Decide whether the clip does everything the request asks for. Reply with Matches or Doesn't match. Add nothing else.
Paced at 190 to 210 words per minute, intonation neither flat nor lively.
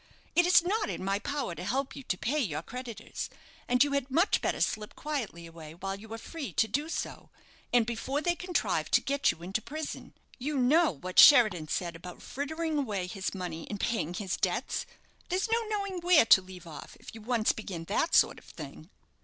Doesn't match